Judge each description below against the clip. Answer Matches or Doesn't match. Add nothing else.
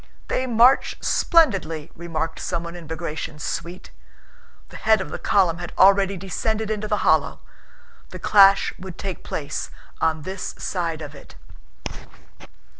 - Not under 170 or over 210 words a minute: Doesn't match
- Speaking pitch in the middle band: Matches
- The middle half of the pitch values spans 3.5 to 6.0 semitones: Matches